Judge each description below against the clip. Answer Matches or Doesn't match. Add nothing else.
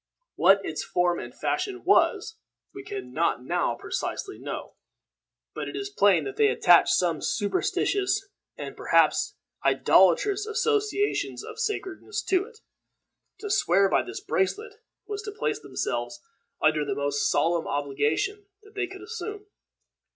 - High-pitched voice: Matches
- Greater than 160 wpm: Doesn't match